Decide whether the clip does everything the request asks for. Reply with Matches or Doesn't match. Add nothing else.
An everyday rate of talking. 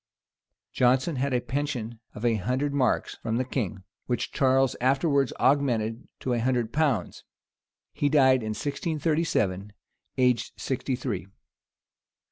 Doesn't match